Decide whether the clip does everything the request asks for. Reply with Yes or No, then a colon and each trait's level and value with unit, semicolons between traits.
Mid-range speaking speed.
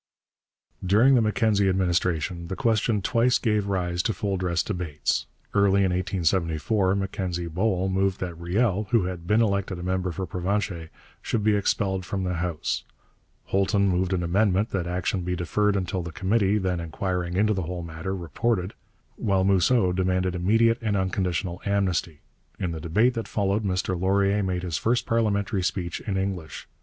Yes: average, 165 wpm